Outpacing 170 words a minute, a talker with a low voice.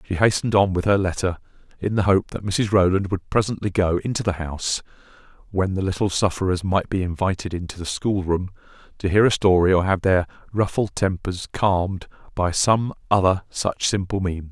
Yes: average, 180 wpm; very low, 95 Hz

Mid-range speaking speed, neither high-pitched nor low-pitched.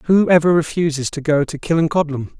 Yes: average, 175 wpm; medium, 155 Hz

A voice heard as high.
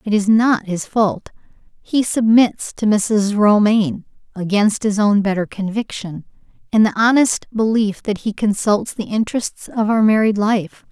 Yes: high, 210 Hz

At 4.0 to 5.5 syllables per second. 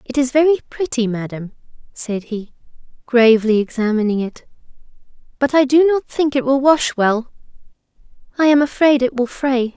Yes: 5.1 syllables/s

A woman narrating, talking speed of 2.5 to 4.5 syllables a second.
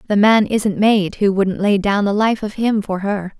Yes: female; 4.4 syllables/s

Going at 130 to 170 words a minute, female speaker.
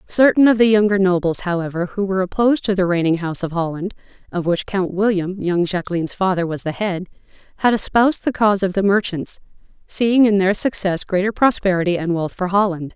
No: average, 195 wpm; female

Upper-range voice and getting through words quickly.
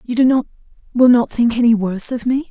Yes: high, 240 Hz; fast, 215 wpm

